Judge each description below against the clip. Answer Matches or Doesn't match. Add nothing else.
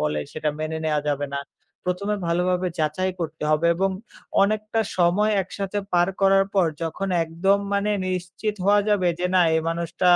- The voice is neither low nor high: Matches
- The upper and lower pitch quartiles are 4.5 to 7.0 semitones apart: Doesn't match